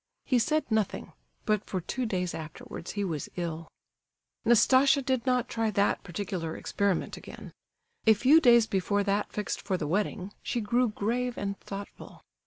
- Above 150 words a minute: Yes, average, 160 wpm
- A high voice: Yes, high, 210 Hz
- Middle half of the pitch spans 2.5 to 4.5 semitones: Yes, average, 4.2 semitones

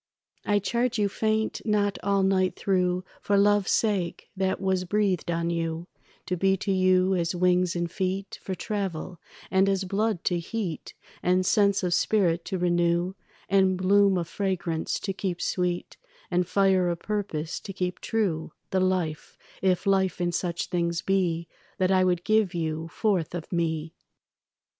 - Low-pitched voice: No, medium, 185 Hz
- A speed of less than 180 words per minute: Yes, average, 160 wpm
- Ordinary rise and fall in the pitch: No, narrow, 2.3 semitones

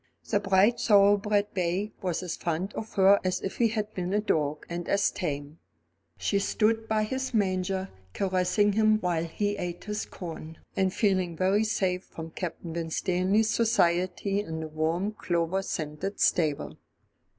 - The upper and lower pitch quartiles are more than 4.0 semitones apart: No, average, 3.3 semitones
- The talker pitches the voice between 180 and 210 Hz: Yes, high, 190 Hz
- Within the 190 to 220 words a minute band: No, average, 155 wpm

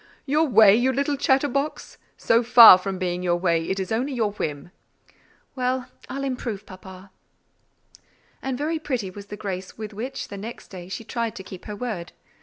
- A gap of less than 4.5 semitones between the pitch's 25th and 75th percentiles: No, average, 5.2 semitones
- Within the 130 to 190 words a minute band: Yes, average, 185 wpm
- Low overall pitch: No, high, 220 Hz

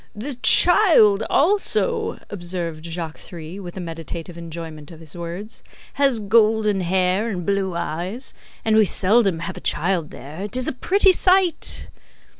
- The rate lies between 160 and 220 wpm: No, average, 150 wpm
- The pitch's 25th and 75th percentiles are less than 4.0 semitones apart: No, average, 5.1 semitones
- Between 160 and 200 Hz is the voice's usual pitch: Yes, high, 190 Hz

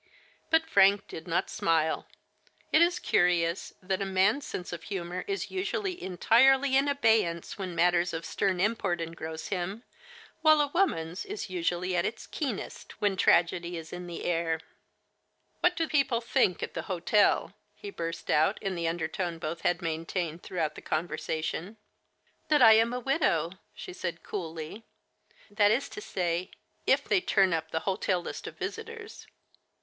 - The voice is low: No, medium, 185 Hz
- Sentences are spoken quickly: No, average, 175 wpm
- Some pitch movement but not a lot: No, wide, 5.8 semitones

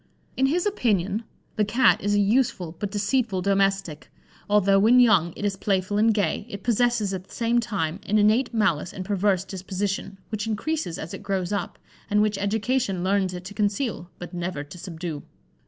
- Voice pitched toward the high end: Yes, high, 200 Hz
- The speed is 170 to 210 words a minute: Yes, average, 185 wpm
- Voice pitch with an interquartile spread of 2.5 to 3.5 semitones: Yes, average, 2.8 semitones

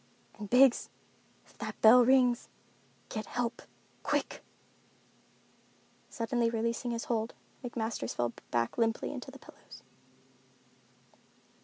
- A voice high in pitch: Yes, high, 230 Hz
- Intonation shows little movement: Yes, narrow, 1.8 semitones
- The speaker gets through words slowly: Yes, slow, 95 wpm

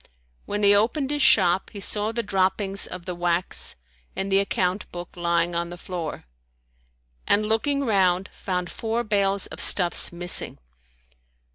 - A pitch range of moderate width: Yes, average, 3.0 semitones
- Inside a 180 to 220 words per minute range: No, average, 150 wpm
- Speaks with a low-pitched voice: No, high, 195 Hz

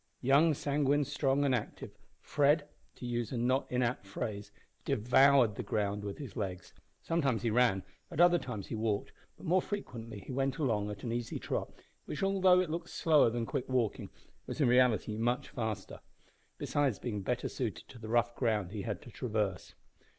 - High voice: No, low, 125 Hz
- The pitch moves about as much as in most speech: Yes, average, 4.5 semitones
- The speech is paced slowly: No, average, 180 wpm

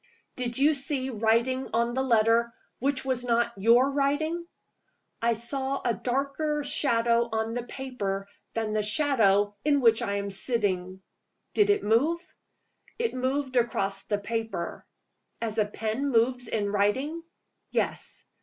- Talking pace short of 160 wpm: Yes, average, 140 wpm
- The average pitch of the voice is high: Yes, high, 235 Hz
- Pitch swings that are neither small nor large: Yes, average, 3.8 semitones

